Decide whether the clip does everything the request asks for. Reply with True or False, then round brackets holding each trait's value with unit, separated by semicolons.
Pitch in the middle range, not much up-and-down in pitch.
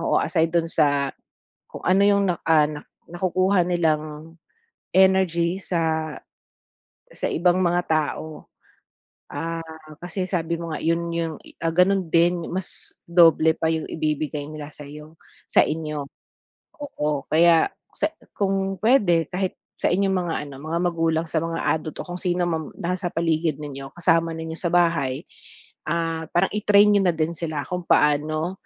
True (165 Hz; 2.2 semitones)